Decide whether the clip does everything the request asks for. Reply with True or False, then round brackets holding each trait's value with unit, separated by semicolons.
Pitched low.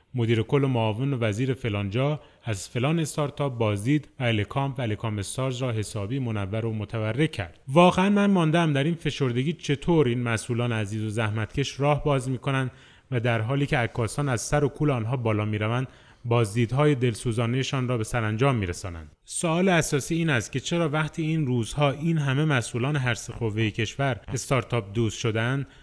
True (130 Hz)